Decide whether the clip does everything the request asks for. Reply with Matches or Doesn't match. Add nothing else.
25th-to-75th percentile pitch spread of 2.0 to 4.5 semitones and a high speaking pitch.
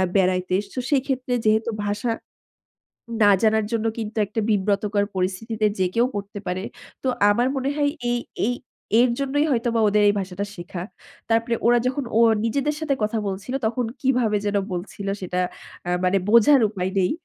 Matches